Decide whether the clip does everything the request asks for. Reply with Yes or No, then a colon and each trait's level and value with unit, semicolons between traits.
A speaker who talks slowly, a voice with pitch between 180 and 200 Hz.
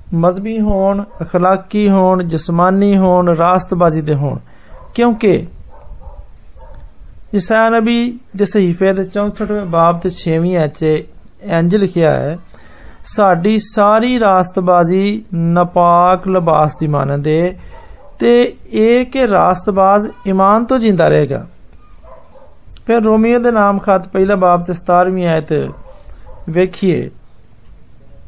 Yes: slow, 105 wpm; medium, 185 Hz